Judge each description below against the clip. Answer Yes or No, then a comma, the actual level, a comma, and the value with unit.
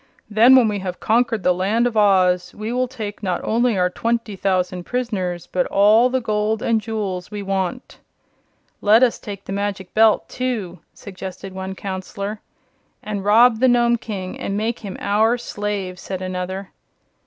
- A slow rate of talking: No, average, 165 wpm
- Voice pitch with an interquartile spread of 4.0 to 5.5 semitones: No, average, 3.3 semitones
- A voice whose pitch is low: No, high, 205 Hz